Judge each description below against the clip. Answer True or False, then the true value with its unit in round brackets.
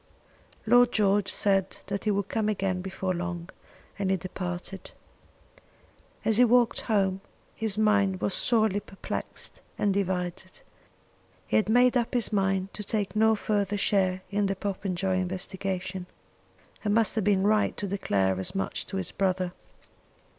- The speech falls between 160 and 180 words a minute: False (150 wpm)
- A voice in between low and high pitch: False (195 Hz)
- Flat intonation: True (2.2 semitones)